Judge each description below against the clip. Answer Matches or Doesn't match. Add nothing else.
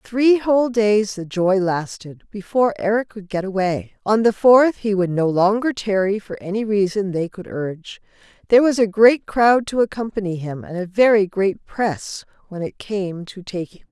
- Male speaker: Doesn't match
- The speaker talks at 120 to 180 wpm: Doesn't match